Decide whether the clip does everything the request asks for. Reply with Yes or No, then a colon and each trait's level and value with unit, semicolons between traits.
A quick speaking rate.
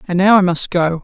Yes: fast, 290 wpm